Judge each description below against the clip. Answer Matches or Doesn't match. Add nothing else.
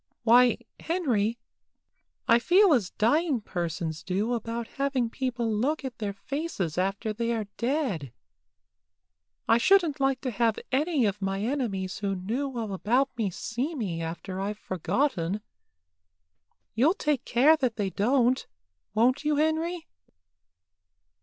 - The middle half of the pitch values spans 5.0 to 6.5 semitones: Matches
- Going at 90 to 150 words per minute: Matches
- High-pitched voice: Matches